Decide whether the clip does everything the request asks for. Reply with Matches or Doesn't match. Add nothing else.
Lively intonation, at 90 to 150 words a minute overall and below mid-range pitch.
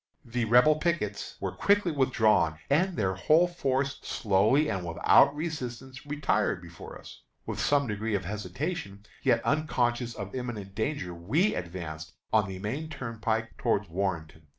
Matches